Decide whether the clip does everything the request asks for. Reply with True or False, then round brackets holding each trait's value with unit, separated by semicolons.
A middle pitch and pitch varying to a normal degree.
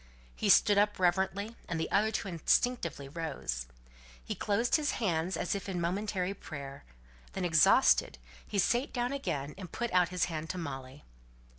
True (180 Hz; 4.4 semitones)